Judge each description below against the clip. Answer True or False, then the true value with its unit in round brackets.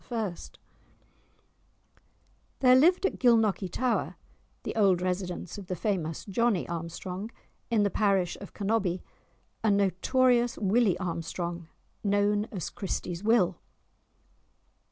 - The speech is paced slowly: True (105 wpm)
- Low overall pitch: False (200 Hz)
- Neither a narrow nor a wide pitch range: True (3.8 semitones)